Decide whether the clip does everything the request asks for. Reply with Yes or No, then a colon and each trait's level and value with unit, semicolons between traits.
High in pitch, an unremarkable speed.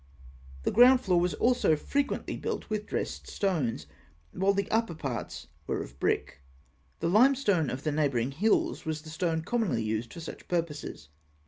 No: medium, 165 Hz; average, 160 wpm